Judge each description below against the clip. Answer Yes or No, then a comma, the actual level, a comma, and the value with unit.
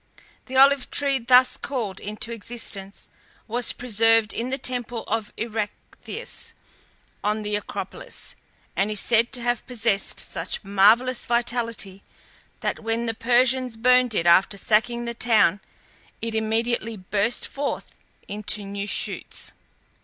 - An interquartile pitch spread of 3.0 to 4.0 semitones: No, narrow, 2.6 semitones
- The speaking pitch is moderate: No, high, 230 Hz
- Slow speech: Yes, slow, 130 wpm